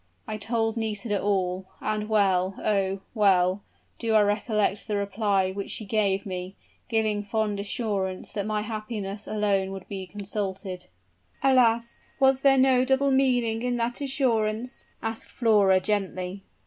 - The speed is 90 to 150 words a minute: Yes, average, 140 wpm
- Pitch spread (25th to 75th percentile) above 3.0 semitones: No, average, 2.7 semitones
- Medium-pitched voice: No, high, 210 Hz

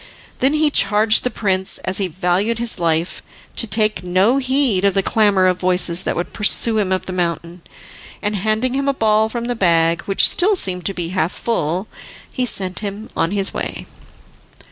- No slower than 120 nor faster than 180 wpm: No, average, 190 wpm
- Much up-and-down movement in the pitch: No, average, 3.7 semitones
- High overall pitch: Yes, high, 200 Hz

